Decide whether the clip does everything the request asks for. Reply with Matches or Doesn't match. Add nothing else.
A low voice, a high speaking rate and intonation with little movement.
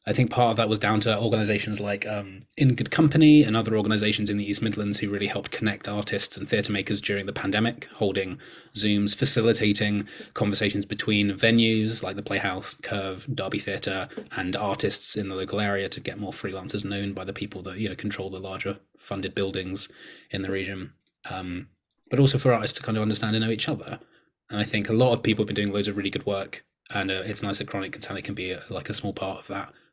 Matches